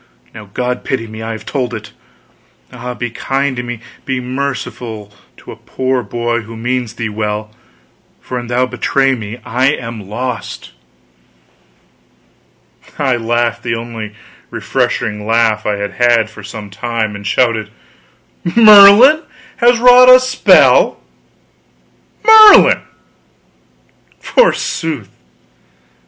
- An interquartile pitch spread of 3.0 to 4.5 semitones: Yes, average, 3.3 semitones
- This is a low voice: Yes, low, 120 Hz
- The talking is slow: Yes, slow, 120 wpm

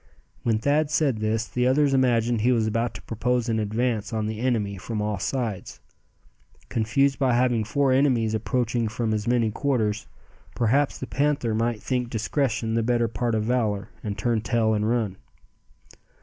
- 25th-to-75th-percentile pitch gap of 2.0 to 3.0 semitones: Yes, narrow, 2.4 semitones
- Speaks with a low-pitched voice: Yes, low, 115 Hz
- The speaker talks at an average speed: Yes, average, 170 wpm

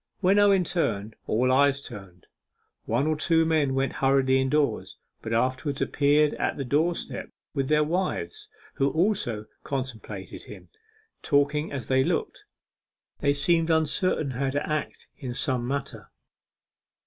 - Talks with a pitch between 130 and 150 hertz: Yes, medium, 140 Hz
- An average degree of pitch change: Yes, average, 3.2 semitones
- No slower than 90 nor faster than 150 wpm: Yes, slow, 135 wpm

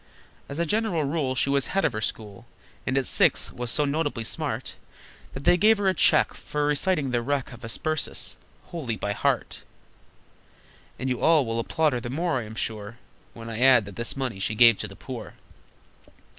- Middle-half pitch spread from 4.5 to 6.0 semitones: Yes, average, 5.2 semitones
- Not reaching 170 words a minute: No, average, 200 wpm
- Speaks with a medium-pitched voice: No, low, 130 Hz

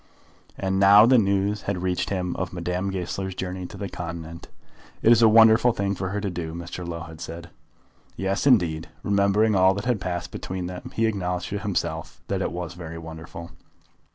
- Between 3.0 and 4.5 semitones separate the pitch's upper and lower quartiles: No, narrow, 2.6 semitones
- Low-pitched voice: Yes, very low, 95 Hz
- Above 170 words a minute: Yes, average, 190 wpm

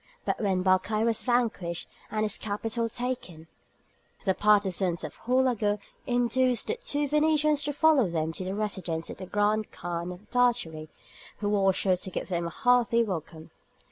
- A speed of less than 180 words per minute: Yes, average, 165 wpm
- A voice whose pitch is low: No, high, 210 Hz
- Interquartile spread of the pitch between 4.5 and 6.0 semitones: Yes, average, 5.1 semitones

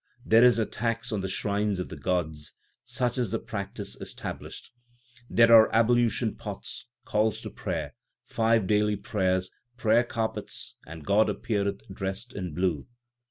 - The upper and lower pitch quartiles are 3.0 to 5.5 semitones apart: Yes, average, 3.3 semitones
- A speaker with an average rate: Yes, average, 150 wpm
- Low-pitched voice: Yes, low, 105 Hz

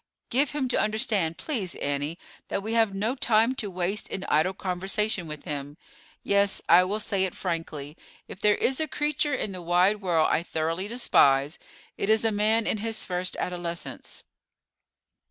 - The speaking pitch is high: Yes, high, 195 Hz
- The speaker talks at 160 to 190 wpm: Yes, average, 170 wpm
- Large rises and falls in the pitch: No, average, 4.3 semitones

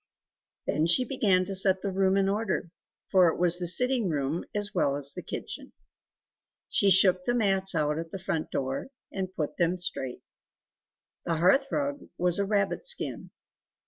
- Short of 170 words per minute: No, average, 175 wpm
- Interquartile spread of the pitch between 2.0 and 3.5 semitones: Yes, average, 3.2 semitones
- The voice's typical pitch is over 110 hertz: Yes, medium, 185 Hz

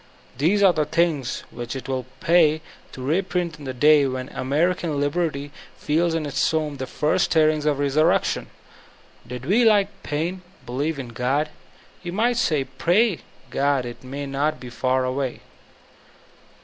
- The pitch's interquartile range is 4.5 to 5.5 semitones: No, average, 4.1 semitones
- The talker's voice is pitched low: No, medium, 150 Hz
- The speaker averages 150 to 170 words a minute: Yes, average, 160 wpm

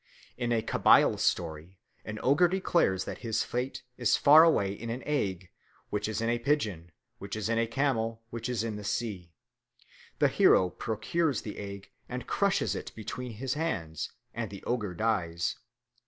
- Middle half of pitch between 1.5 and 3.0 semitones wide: No, average, 4.1 semitones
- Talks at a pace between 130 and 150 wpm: No, average, 170 wpm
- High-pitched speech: No, low, 110 Hz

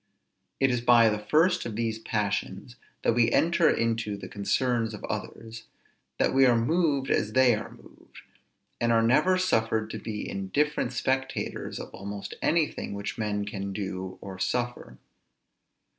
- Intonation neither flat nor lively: Yes, average, 3.9 semitones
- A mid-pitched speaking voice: No, low, 115 Hz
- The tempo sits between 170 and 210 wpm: No, average, 155 wpm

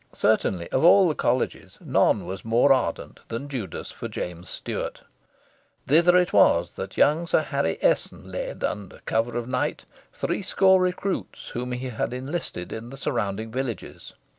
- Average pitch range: No, wide, 5.9 semitones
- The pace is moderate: Yes, average, 160 wpm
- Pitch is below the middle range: Yes, low, 125 Hz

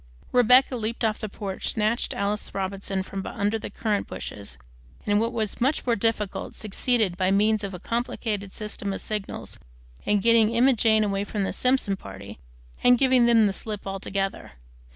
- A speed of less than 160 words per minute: No, average, 175 wpm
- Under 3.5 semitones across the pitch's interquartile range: Yes, average, 2.8 semitones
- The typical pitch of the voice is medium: No, high, 210 Hz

